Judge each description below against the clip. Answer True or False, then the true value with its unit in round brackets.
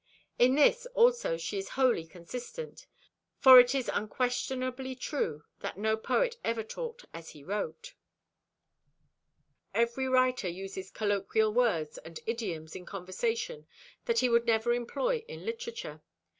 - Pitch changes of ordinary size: False (6.9 semitones)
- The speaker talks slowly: True (130 wpm)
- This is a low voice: False (240 Hz)